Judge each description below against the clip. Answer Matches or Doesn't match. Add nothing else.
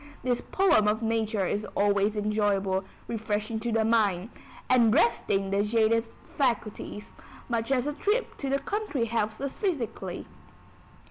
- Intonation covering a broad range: Doesn't match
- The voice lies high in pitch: Matches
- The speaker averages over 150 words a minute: Doesn't match